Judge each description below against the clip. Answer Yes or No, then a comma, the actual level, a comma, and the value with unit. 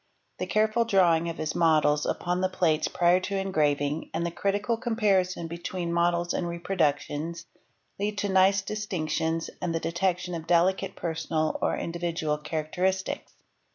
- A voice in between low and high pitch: Yes, medium, 175 Hz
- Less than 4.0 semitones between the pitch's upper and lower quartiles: Yes, average, 2.8 semitones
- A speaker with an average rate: Yes, average, 150 wpm